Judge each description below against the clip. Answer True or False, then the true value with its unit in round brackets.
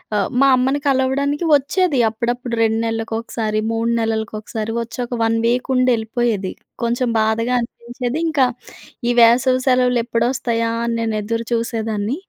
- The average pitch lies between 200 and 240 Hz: True (235 Hz)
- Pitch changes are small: True (2.1 semitones)